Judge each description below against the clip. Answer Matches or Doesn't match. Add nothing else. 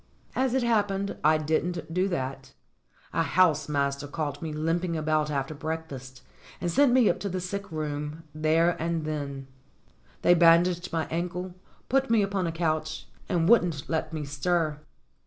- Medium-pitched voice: Matches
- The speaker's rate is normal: Matches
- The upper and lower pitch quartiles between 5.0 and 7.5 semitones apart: Doesn't match